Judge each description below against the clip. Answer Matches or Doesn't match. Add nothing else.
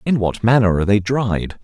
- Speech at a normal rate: Doesn't match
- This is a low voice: Matches